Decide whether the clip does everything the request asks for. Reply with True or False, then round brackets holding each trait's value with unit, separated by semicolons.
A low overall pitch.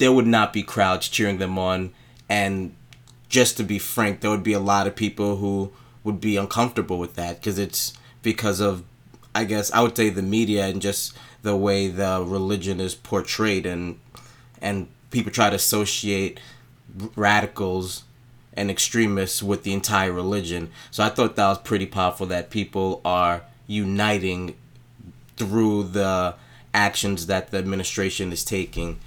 True (100 Hz)